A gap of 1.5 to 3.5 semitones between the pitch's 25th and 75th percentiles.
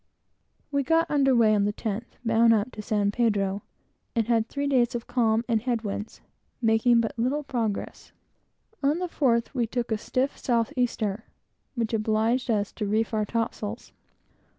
Yes: narrow, 2.5 semitones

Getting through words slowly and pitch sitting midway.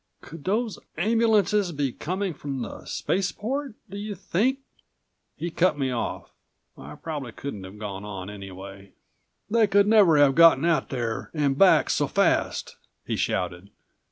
No: average, 155 wpm; medium, 155 Hz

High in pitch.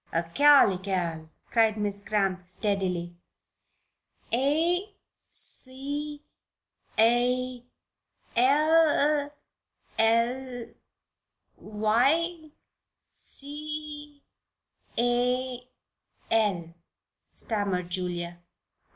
Yes: high, 240 Hz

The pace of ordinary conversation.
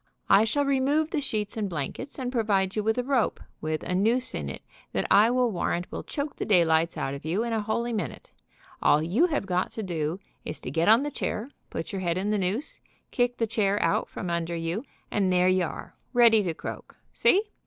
No: fast, 225 wpm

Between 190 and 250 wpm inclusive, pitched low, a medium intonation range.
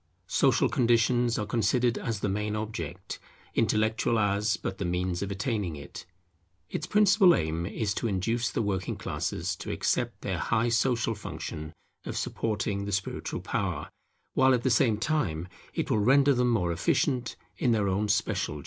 No: average, 165 wpm; low, 110 Hz; average, 3.5 semitones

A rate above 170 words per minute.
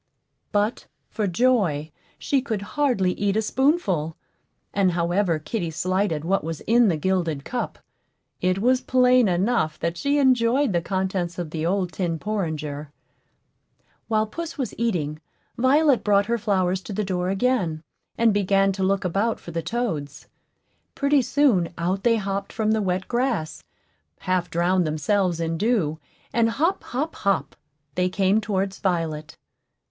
No: average, 150 wpm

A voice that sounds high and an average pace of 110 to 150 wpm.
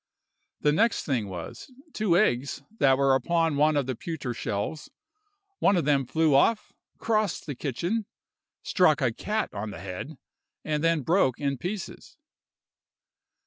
No: medium, 150 Hz; average, 145 wpm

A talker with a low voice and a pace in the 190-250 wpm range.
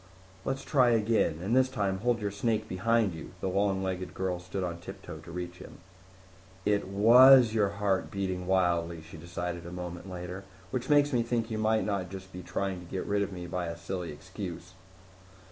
Yes: very low, 95 Hz; average, 195 wpm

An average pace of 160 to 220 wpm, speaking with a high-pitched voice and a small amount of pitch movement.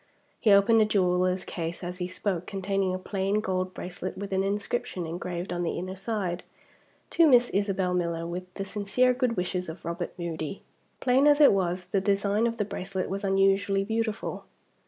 Yes: average, 180 wpm; high, 195 Hz; narrow, 2.3 semitones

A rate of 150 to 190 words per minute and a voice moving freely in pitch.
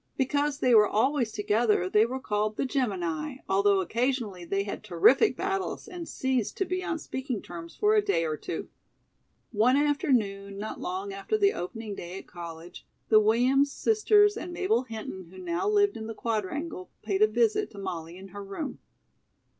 Yes: average, 180 wpm; wide, 6.5 semitones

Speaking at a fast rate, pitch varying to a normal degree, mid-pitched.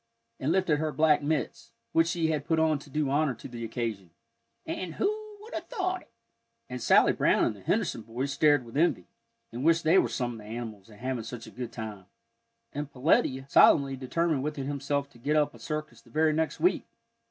Yes: fast, 210 wpm; average, 4.6 semitones; medium, 145 Hz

